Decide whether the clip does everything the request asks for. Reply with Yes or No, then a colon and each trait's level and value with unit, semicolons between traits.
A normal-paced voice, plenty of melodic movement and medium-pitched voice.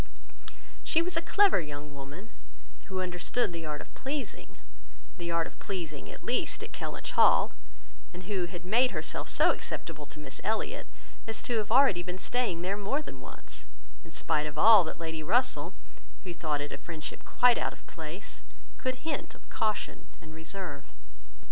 Yes: average, 175 wpm; wide, 6.2 semitones; medium, 180 Hz